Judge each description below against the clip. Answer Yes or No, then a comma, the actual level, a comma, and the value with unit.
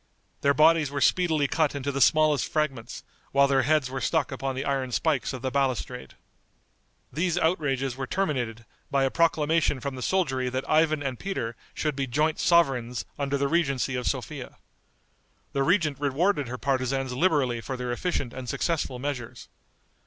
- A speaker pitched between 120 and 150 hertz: Yes, medium, 140 Hz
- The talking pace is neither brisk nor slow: Yes, average, 165 wpm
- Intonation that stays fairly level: No, average, 3.1 semitones